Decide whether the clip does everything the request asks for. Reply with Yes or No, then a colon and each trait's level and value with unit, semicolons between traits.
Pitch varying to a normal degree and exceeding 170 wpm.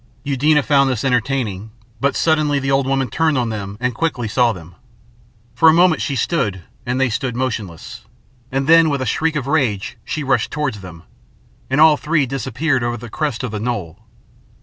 Yes: average, 4.6 semitones; average, 190 wpm